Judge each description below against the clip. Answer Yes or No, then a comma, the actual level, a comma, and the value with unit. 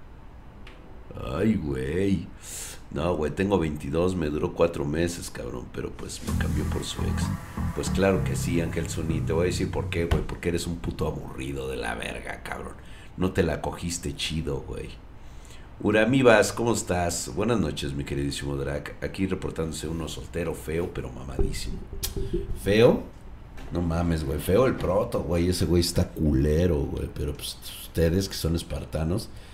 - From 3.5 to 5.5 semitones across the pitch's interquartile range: Yes, average, 3.8 semitones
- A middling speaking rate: Yes, average, 160 wpm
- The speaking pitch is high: No, very low, 85 Hz